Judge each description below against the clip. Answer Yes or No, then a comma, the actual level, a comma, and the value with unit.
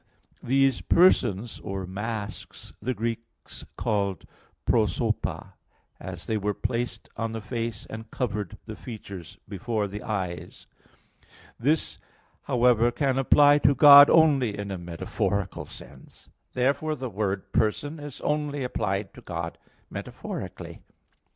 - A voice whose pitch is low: Yes, low, 115 Hz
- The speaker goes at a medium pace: No, slow, 120 wpm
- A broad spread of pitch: No, average, 5.0 semitones